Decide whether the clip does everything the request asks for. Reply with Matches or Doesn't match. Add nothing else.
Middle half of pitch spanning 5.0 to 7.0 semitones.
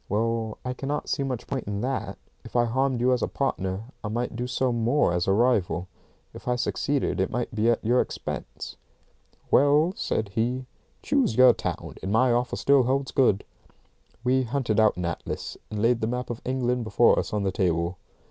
Doesn't match